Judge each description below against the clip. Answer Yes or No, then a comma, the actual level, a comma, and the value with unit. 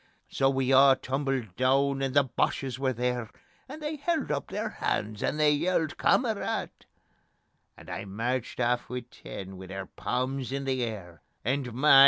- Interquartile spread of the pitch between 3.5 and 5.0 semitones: No, narrow, 2.6 semitones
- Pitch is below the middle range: Yes, low, 130 Hz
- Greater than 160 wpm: Yes, average, 170 wpm